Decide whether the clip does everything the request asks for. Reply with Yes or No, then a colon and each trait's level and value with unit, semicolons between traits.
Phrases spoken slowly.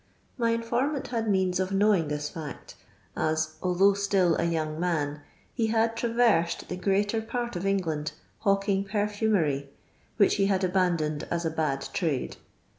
No: average, 160 wpm